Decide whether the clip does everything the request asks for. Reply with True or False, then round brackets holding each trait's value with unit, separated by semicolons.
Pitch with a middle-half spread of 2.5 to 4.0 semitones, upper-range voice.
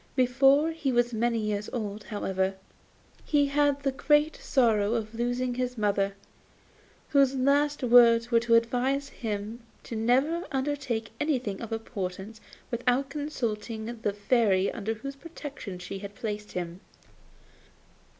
False (4.4 semitones; 235 Hz)